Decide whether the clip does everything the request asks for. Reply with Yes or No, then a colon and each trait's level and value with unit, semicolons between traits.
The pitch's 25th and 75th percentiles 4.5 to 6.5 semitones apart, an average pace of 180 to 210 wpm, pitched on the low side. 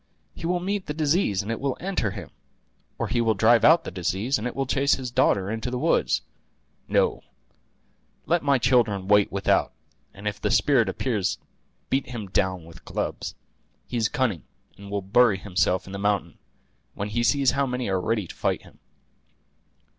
Yes: average, 5.2 semitones; average, 185 wpm; low, 115 Hz